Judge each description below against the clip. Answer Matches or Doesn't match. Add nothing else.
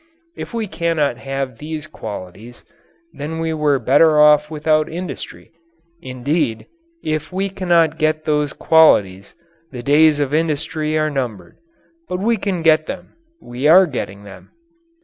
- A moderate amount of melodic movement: Matches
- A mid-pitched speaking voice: Matches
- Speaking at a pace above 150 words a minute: Doesn't match